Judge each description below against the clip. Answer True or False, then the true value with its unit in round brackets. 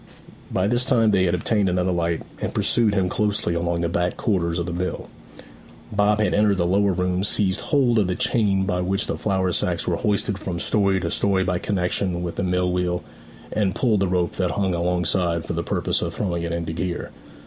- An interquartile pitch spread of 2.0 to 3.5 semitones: True (2.6 semitones)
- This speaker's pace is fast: True (215 wpm)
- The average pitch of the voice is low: True (90 Hz)